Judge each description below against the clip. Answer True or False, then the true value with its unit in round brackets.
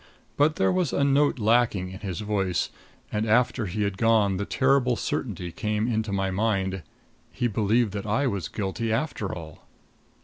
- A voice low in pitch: True (105 Hz)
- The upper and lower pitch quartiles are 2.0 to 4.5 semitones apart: True (4.0 semitones)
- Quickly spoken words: False (170 wpm)